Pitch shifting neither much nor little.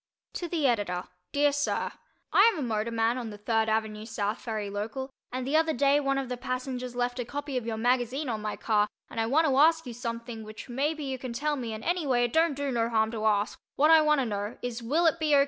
Yes: average, 4.3 semitones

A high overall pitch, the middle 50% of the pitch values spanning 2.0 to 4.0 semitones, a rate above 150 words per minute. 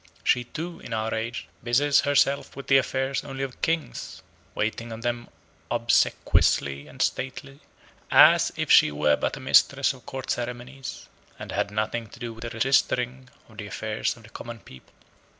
No: low, 120 Hz; average, 3.2 semitones; average, 170 wpm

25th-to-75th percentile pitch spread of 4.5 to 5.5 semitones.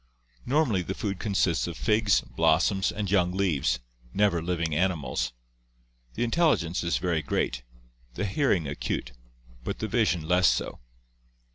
No: average, 4.0 semitones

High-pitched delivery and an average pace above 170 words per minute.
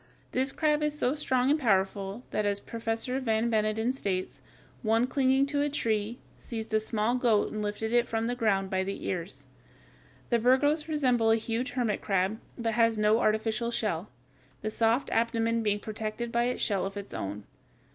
Yes: high, 225 Hz; average, 180 wpm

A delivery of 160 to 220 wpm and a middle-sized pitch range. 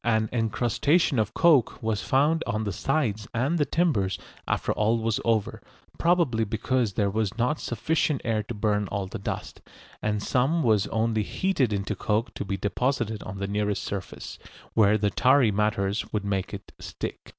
Yes: average, 175 wpm; average, 3.7 semitones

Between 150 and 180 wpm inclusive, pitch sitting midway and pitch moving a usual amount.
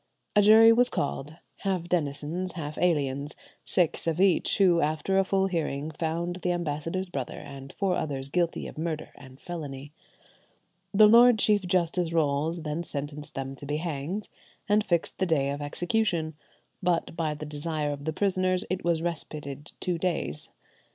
Yes: average, 160 wpm; medium, 165 Hz; average, 3.8 semitones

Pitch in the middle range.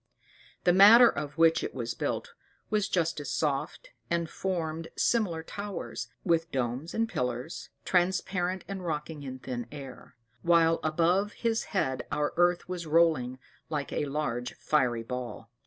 Yes: medium, 165 Hz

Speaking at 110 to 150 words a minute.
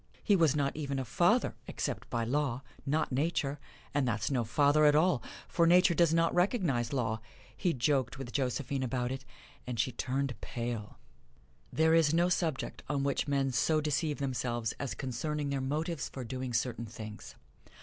No: average, 170 wpm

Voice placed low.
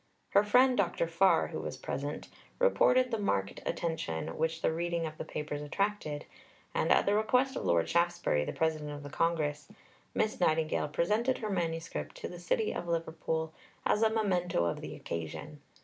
No: medium, 170 Hz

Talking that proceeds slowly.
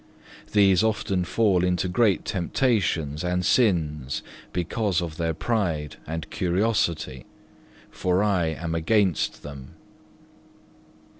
Yes: slow, 100 wpm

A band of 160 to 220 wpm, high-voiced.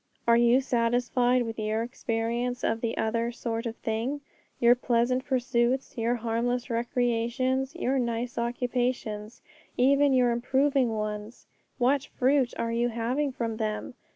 No: slow, 135 wpm; high, 240 Hz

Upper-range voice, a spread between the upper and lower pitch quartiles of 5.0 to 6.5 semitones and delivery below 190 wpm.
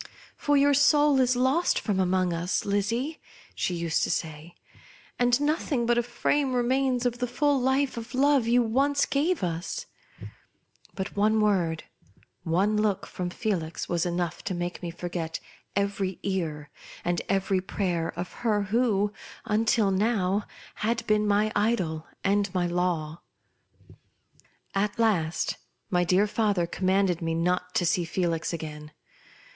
Yes: high, 200 Hz; average, 5.3 semitones; average, 145 wpm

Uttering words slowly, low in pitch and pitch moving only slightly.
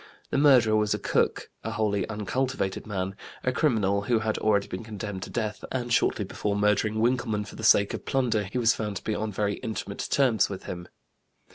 No: fast, 205 wpm; low, 110 Hz; narrow, 2.3 semitones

